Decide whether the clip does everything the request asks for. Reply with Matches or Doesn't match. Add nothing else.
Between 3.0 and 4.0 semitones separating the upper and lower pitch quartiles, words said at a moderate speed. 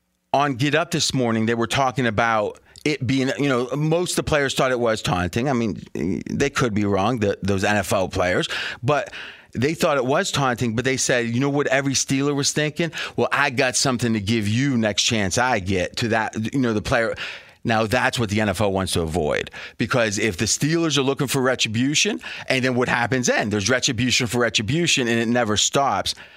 Doesn't match